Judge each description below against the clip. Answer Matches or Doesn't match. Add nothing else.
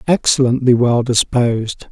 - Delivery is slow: Matches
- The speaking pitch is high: Doesn't match